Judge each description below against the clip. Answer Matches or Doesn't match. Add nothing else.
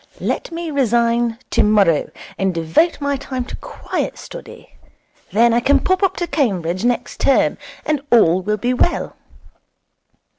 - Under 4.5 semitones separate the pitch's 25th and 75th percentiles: Doesn't match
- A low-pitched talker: Doesn't match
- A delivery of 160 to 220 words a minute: Doesn't match